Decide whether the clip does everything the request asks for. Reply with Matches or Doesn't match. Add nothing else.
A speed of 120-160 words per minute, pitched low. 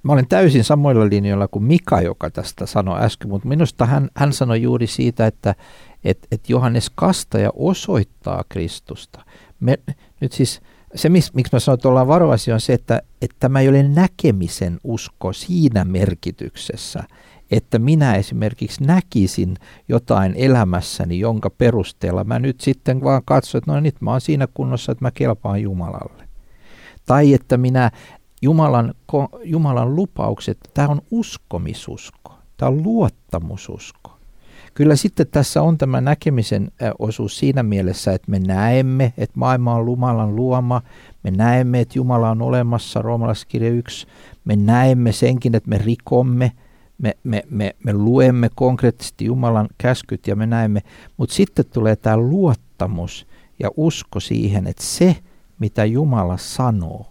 Matches